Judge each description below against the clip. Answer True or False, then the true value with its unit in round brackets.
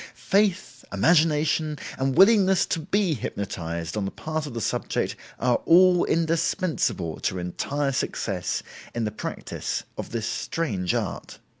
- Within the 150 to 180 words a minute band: False (135 wpm)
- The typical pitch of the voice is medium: True (150 Hz)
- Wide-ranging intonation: True (8.5 semitones)